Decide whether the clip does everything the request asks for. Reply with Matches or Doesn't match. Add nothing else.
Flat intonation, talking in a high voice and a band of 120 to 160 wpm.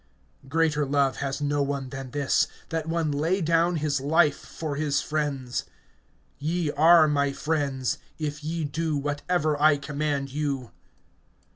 Doesn't match